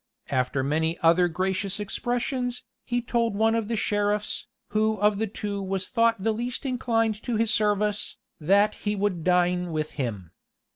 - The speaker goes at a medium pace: Yes, average, 160 wpm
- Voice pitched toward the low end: No, high, 205 Hz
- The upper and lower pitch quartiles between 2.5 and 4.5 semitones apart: Yes, average, 3.9 semitones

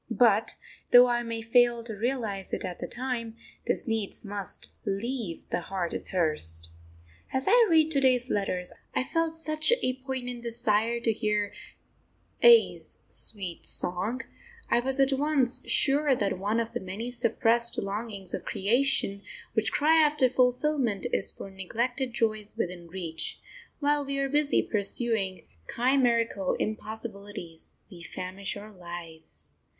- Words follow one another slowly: No, average, 145 wpm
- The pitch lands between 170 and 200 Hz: No, high, 230 Hz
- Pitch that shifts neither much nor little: Yes, average, 4.7 semitones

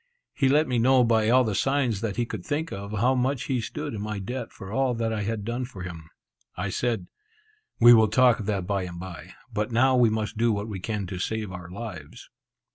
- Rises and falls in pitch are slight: No, average, 3.7 semitones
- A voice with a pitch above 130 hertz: No, low, 110 Hz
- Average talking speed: No, fast, 235 wpm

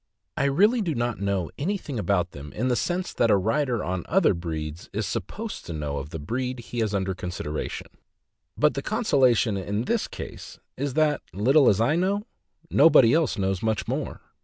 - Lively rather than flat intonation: Yes, wide, 7.2 semitones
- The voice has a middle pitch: No, low, 115 Hz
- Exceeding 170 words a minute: Yes, average, 185 wpm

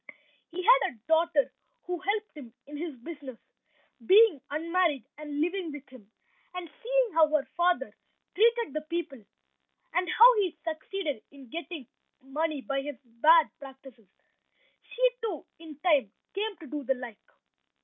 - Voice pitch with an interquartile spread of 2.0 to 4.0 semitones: No, average, 4.7 semitones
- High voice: Yes, very high, 315 Hz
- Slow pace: No, average, 150 wpm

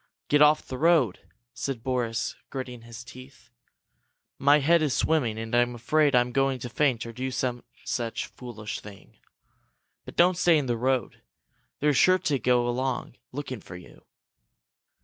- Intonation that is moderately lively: Yes, average, 3.2 semitones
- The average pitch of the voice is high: No, low, 125 Hz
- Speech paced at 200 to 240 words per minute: No, average, 160 wpm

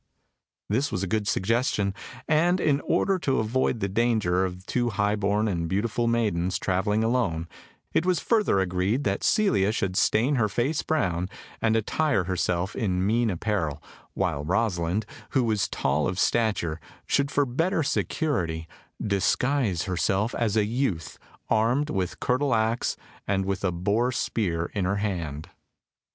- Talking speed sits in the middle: Yes, average, 150 wpm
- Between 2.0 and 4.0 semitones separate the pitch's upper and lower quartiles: No, average, 4.7 semitones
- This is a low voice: Yes, low, 105 Hz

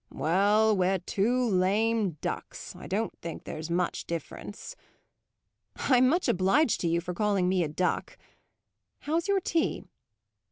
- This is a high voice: Yes, high, 195 Hz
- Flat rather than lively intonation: No, average, 4.3 semitones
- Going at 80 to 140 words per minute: Yes, slow, 135 wpm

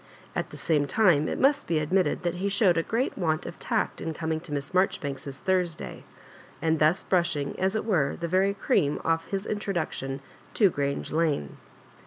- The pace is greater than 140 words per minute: Yes, average, 185 wpm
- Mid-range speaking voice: Yes, medium, 165 Hz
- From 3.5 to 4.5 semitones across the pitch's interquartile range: Yes, average, 4.0 semitones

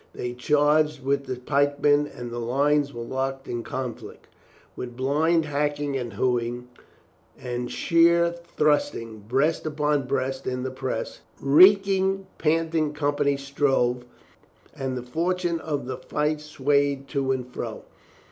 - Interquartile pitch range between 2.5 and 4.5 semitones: Yes, average, 2.9 semitones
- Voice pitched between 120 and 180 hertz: Yes, medium, 140 Hz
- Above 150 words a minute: No, average, 140 wpm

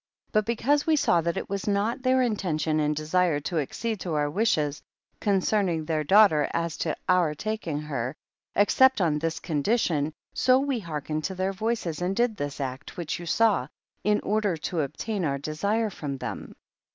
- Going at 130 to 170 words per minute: No, average, 180 wpm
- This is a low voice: No, medium, 175 Hz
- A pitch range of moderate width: No, wide, 5.8 semitones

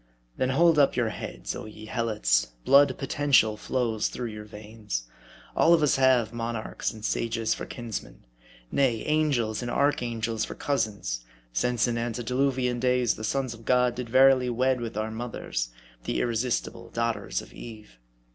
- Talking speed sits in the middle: Yes, average, 155 wpm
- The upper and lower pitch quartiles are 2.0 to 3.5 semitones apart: Yes, average, 2.9 semitones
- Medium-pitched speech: No, low, 120 Hz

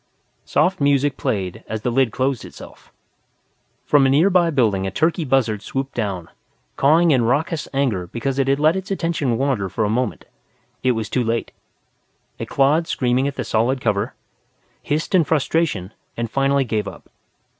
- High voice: No, low, 135 Hz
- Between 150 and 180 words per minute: Yes, average, 165 wpm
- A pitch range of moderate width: Yes, average, 4.6 semitones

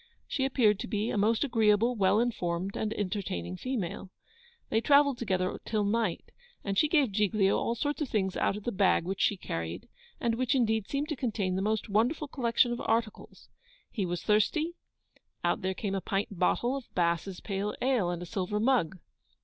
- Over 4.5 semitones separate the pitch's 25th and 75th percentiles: No, average, 3.9 semitones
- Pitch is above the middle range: Yes, high, 210 Hz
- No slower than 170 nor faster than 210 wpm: Yes, average, 190 wpm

